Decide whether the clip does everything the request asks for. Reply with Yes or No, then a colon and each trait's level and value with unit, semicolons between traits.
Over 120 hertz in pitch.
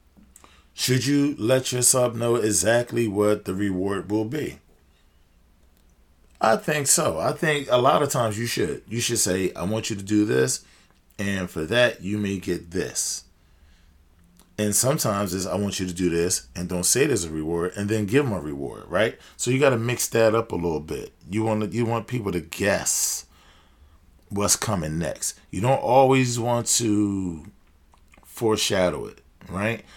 No: low, 100 Hz